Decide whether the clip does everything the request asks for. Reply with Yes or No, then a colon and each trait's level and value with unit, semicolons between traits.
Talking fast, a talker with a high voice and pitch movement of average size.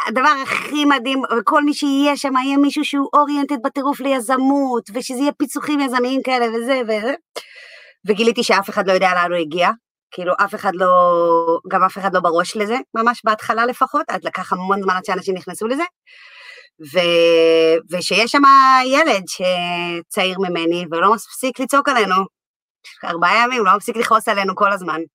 No: fast, 160 wpm; high, 225 Hz; wide, 6.8 semitones